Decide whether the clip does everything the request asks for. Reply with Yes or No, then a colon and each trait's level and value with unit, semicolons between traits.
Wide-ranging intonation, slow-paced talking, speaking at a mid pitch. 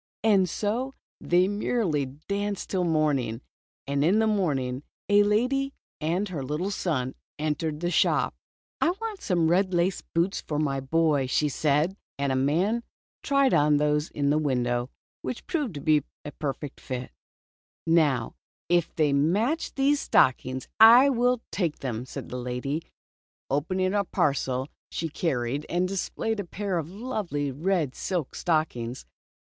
No: wide, 6.3 semitones; average, 155 wpm; medium, 165 Hz